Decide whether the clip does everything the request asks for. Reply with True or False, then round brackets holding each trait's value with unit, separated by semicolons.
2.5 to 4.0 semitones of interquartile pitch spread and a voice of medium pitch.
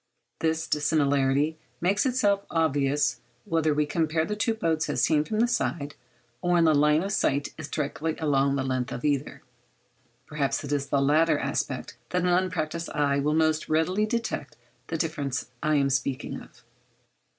True (2.8 semitones; 155 Hz)